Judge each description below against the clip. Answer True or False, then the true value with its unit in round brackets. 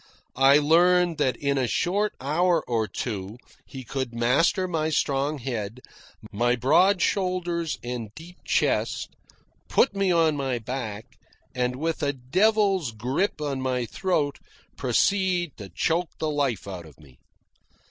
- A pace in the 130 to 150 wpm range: True (140 wpm)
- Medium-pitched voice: True (145 Hz)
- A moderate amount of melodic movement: False (6.2 semitones)